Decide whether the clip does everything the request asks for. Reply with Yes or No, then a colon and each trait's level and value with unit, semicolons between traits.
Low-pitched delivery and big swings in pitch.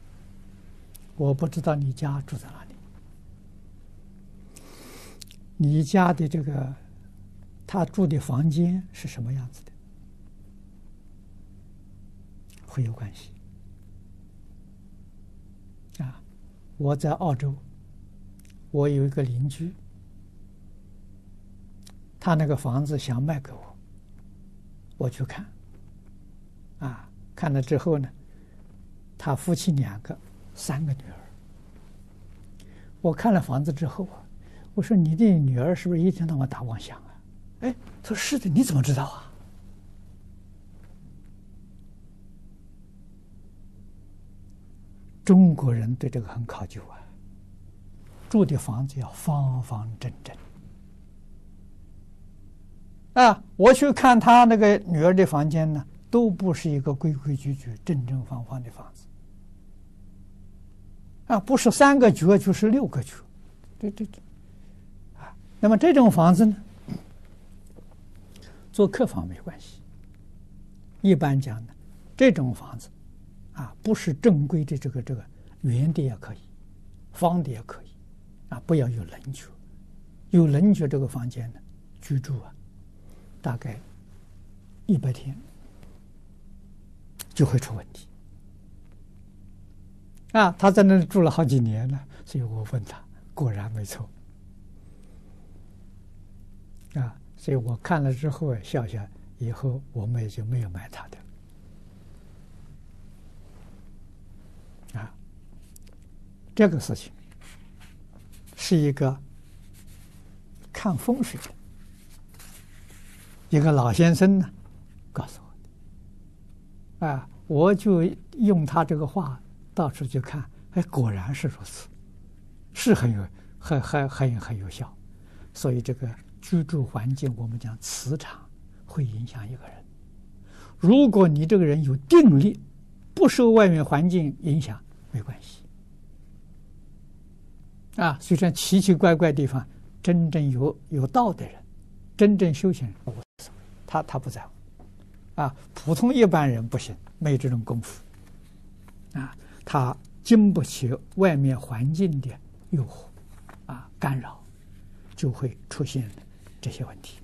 Yes: low, 100 Hz; wide, 7.2 semitones